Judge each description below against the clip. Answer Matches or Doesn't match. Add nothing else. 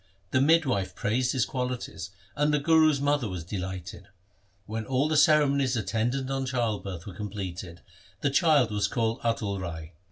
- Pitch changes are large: Matches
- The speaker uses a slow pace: Doesn't match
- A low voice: Matches